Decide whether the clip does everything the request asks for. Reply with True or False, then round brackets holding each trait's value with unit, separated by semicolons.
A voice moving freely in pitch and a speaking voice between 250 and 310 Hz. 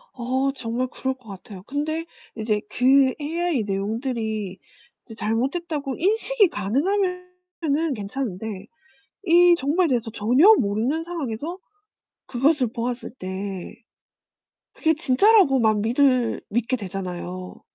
True (6.8 semitones; 255 Hz)